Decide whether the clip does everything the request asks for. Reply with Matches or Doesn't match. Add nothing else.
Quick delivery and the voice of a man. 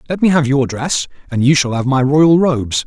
Matches